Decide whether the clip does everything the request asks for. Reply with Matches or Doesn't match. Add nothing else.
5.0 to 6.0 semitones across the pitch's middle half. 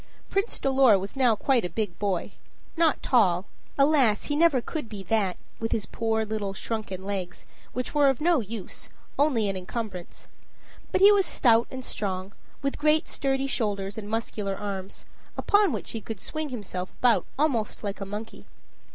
Matches